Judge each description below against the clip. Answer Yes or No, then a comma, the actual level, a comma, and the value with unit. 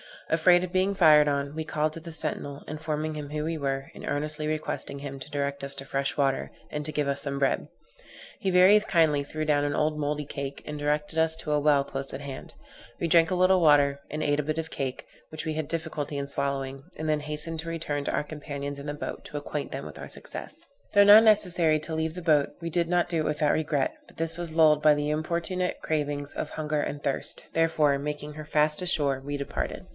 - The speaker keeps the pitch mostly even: Yes, narrow, 2.1 semitones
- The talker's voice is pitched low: No, medium, 150 Hz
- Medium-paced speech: No, fast, 235 wpm